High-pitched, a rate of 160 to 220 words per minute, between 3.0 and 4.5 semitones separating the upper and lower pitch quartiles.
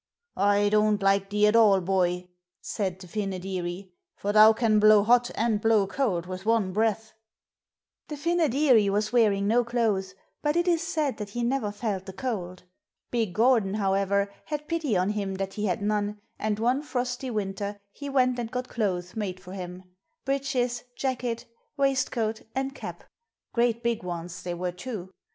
Yes: high, 215 Hz; average, 170 wpm; average, 3.9 semitones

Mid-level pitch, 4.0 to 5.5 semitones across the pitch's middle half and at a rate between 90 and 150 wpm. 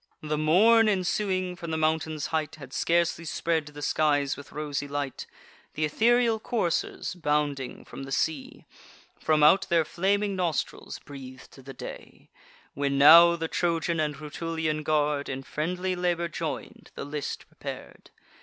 No: medium, 155 Hz; average, 3.0 semitones; average, 145 wpm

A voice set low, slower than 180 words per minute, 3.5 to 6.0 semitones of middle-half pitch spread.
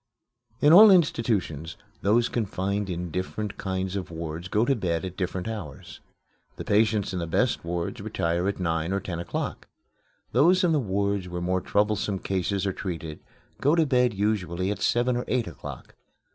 Yes: low, 100 Hz; average, 170 wpm; average, 4.2 semitones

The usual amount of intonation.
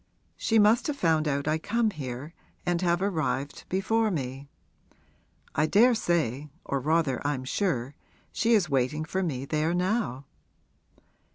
No: wide, 5.9 semitones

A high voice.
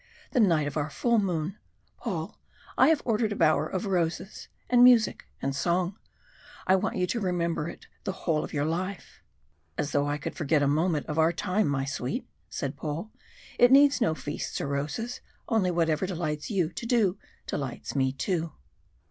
No: medium, 170 Hz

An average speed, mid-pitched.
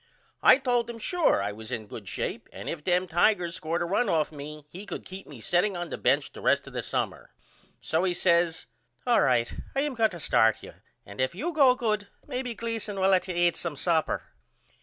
No: fast, 225 wpm; medium, 180 Hz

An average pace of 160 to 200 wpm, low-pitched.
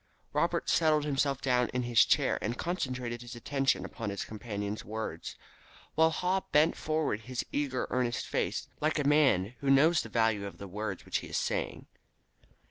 Yes: average, 175 wpm; low, 125 Hz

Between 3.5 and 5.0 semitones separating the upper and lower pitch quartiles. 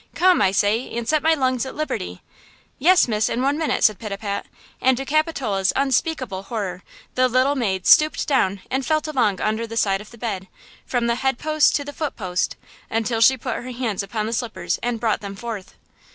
Yes: average, 4.6 semitones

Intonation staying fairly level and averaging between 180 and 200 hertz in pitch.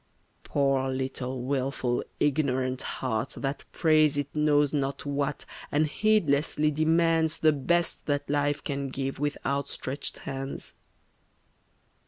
No: narrow, 2.0 semitones; medium, 140 Hz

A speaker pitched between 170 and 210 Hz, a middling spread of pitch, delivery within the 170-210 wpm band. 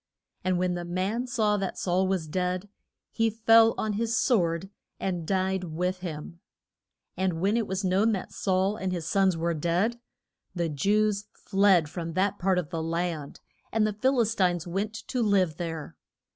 Yes: medium, 185 Hz; average, 3.2 semitones; average, 175 wpm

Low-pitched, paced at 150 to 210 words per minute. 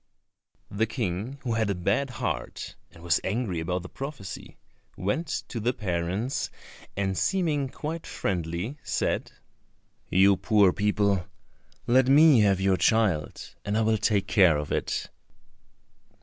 No: low, 105 Hz; slow, 135 wpm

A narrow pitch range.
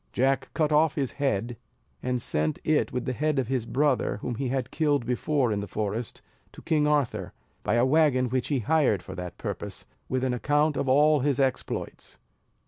No: average, 3.6 semitones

